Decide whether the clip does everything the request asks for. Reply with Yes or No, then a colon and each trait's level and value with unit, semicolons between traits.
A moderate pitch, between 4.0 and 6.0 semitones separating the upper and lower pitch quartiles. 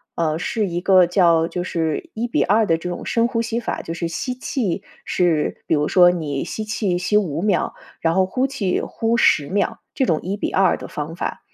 Yes: medium, 180 Hz; average, 4.6 semitones